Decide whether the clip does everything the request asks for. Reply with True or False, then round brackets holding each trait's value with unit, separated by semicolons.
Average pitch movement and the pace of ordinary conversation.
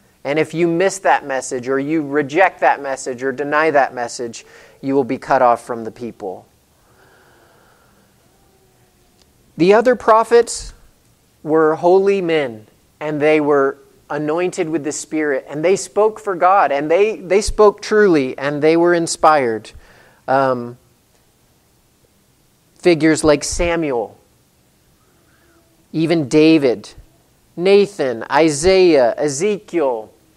False (5.0 semitones; 115 wpm)